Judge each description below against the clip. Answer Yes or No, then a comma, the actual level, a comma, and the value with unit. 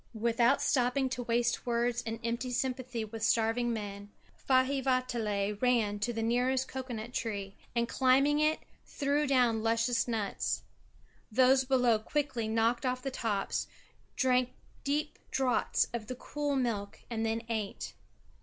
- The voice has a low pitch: No, high, 240 Hz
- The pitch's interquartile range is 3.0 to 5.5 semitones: No, narrow, 2.4 semitones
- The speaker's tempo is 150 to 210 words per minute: No, average, 140 wpm